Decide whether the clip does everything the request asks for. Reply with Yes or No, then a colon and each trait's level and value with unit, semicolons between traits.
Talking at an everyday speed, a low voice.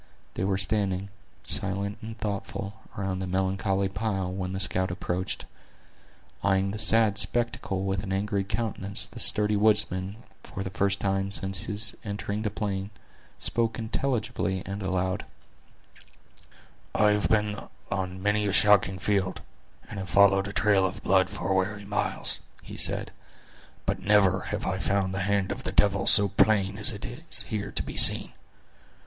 Yes: average, 160 wpm; low, 100 Hz